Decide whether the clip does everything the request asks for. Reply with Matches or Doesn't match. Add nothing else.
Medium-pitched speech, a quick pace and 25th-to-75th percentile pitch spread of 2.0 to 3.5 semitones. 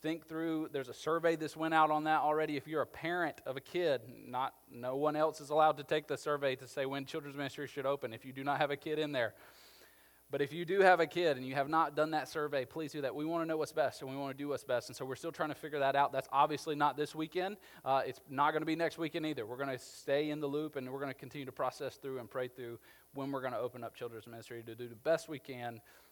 Matches